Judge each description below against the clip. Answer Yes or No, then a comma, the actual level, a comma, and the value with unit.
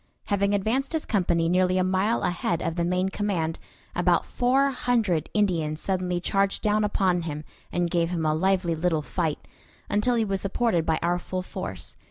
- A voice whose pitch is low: No, medium, 185 Hz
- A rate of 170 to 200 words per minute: Yes, average, 180 wpm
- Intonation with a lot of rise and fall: No, average, 3.4 semitones